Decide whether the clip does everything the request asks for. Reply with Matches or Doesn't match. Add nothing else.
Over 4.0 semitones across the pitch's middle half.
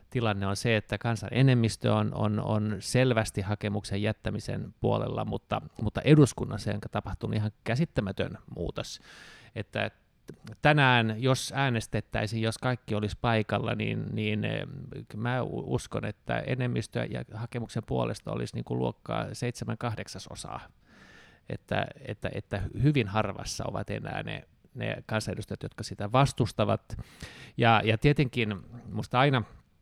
Doesn't match